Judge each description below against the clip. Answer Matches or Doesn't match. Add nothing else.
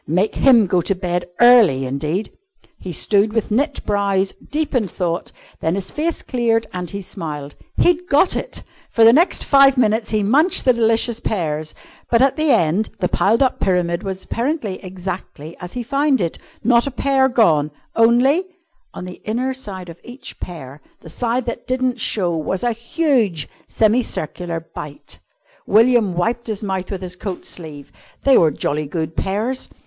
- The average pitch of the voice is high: Matches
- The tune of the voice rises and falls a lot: Matches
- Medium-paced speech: Matches